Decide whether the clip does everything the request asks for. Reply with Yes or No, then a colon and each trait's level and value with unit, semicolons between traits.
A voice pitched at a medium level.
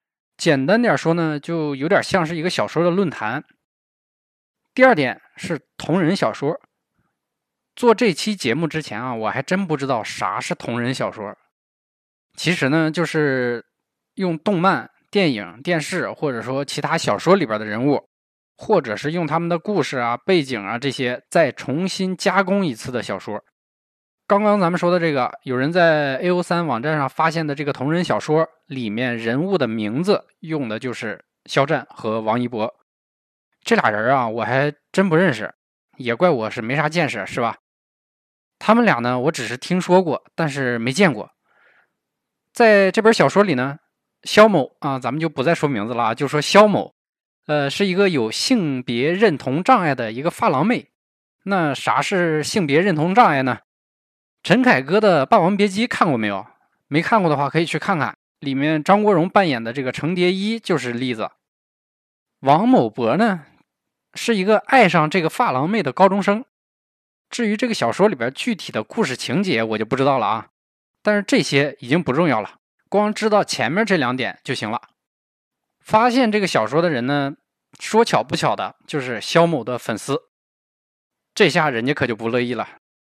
Yes: medium, 160 Hz